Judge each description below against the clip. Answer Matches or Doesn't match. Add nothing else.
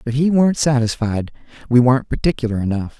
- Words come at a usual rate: Matches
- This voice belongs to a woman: Doesn't match